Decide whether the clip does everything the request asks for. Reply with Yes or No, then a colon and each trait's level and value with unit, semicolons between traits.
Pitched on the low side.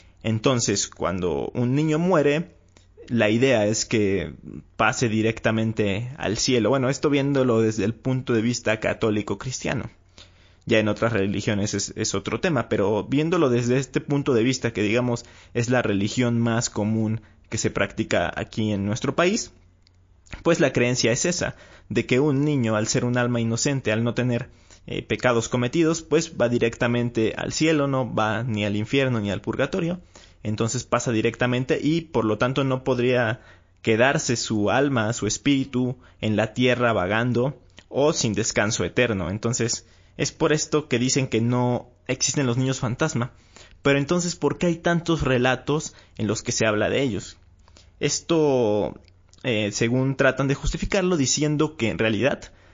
Yes: low, 120 Hz